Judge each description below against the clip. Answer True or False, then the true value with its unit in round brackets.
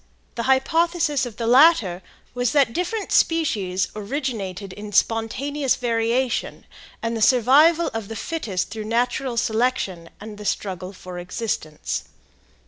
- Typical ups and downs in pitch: True (4.8 semitones)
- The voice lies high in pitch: True (230 Hz)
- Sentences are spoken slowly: True (130 wpm)